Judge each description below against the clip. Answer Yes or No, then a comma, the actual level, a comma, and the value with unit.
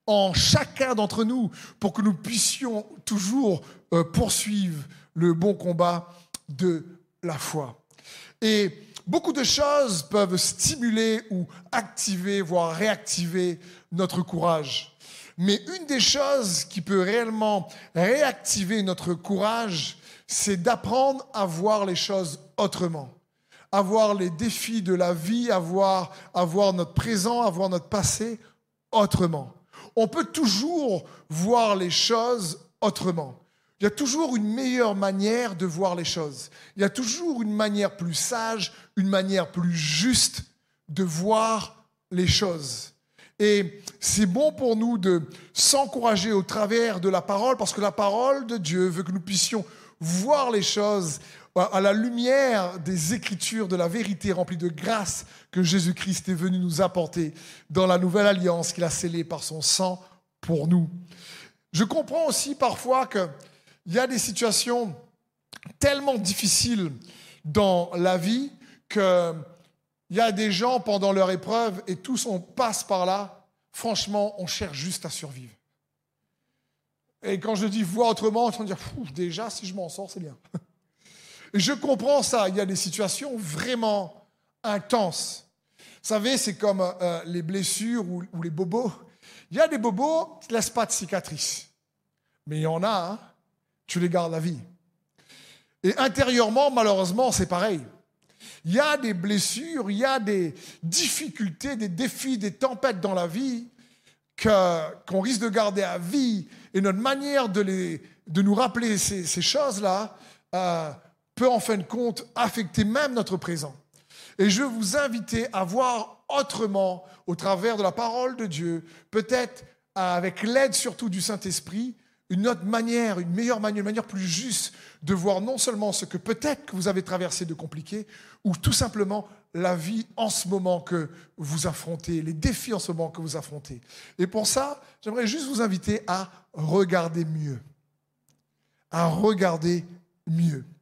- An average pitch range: Yes, average, 4.4 semitones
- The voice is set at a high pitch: Yes, high, 195 Hz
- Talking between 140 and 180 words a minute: Yes, average, 160 wpm